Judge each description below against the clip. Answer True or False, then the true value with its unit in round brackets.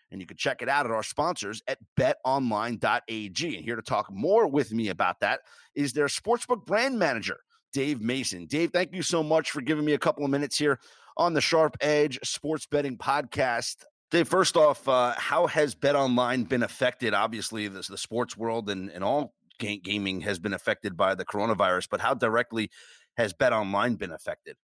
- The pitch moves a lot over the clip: True (5.8 semitones)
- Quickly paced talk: False (190 wpm)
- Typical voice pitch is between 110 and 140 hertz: True (135 Hz)